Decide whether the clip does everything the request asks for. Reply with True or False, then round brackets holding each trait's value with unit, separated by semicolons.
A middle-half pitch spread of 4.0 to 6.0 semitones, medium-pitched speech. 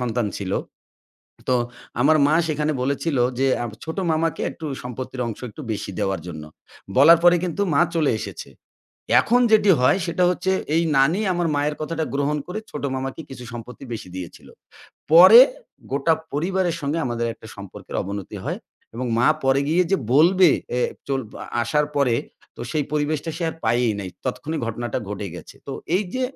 True (5.3 semitones; 145 Hz)